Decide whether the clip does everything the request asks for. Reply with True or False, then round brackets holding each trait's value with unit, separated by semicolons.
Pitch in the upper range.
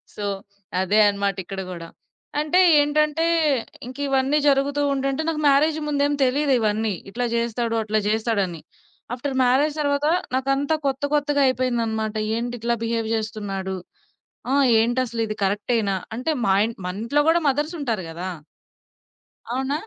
True (245 Hz)